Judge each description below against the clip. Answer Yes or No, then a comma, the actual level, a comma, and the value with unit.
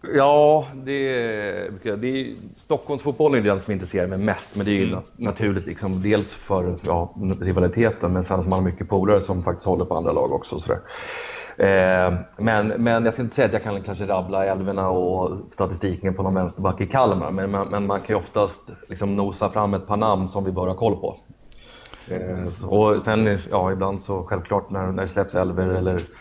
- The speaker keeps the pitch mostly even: Yes, narrow, 2.2 semitones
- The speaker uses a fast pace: Yes, fast, 205 wpm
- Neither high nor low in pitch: No, low, 100 Hz